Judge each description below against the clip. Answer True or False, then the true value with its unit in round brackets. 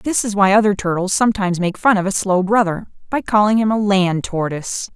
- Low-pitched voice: False (200 Hz)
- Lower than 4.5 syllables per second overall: False (5.8 syllables/s)